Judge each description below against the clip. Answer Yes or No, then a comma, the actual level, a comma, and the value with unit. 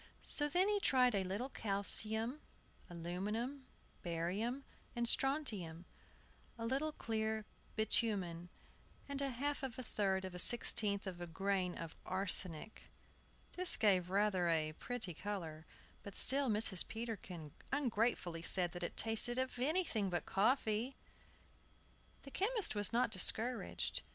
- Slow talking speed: Yes, slow, 130 wpm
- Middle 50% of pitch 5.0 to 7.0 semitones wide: Yes, wide, 5.5 semitones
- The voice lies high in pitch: Yes, high, 215 Hz